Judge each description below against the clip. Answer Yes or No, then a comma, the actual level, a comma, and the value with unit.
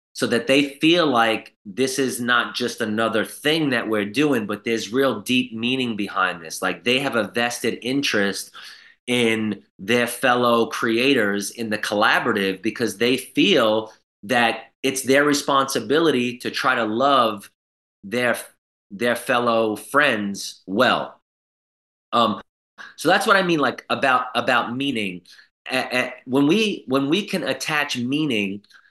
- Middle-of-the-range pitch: No, low, 120 Hz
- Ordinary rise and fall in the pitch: Yes, average, 3.7 semitones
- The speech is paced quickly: No, average, 145 wpm